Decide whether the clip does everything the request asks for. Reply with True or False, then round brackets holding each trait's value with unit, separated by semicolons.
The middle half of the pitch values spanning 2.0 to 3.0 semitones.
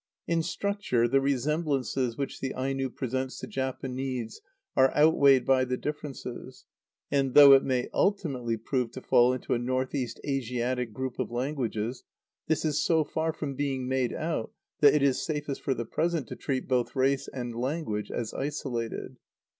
True (2.5 semitones)